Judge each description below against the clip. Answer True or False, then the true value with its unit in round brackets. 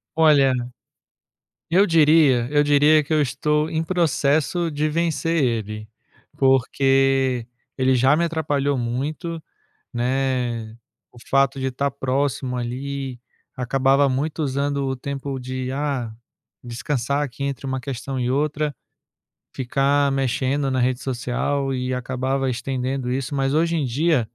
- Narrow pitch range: True (2.3 semitones)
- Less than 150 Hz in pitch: True (135 Hz)